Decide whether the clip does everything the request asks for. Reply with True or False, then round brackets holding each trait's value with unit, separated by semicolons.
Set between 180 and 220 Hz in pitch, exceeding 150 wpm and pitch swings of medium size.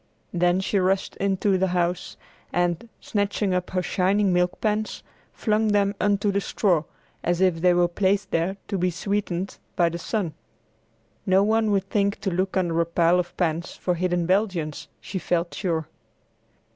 False (185 Hz; 170 wpm; 2.3 semitones)